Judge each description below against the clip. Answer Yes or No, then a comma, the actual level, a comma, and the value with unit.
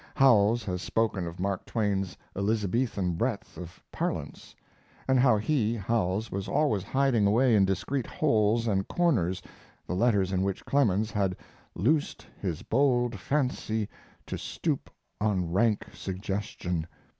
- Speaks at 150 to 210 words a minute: No, slow, 135 wpm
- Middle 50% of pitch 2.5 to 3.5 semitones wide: No, average, 4.0 semitones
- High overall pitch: No, low, 105 Hz